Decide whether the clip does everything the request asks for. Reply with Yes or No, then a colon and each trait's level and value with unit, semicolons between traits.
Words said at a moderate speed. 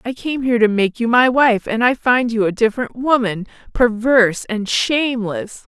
Yes: average, 190 wpm